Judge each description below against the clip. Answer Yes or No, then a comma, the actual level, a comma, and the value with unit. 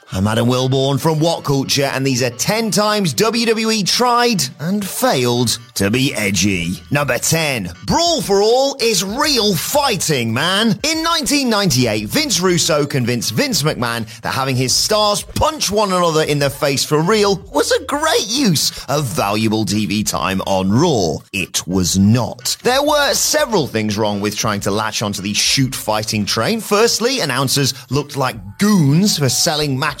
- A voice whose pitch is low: No, medium, 145 Hz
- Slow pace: No, average, 160 wpm